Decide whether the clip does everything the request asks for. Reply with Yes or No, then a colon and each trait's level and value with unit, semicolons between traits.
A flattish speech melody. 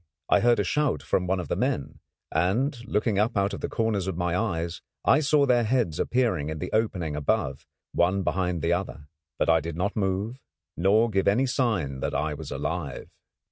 No: wide, 5.4 semitones